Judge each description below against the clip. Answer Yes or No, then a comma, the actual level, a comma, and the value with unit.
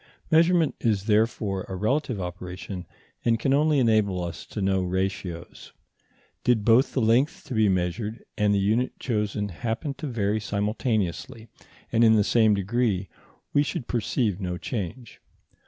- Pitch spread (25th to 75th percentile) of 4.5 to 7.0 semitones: No, average, 3.8 semitones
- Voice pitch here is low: Yes, low, 110 Hz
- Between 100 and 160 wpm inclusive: Yes, average, 150 wpm